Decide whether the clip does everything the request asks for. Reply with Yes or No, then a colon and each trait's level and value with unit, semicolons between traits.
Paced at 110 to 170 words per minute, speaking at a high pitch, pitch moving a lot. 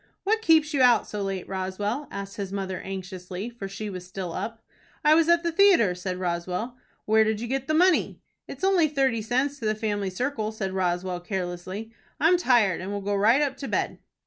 No: fast, 205 wpm; high, 215 Hz; wide, 6.3 semitones